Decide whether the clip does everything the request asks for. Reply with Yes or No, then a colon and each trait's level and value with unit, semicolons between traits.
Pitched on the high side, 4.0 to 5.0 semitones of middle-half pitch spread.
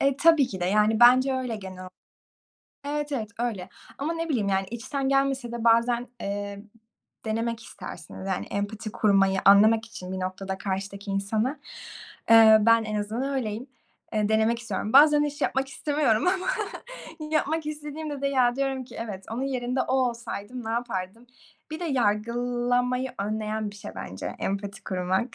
Yes: high, 230 Hz; average, 4.5 semitones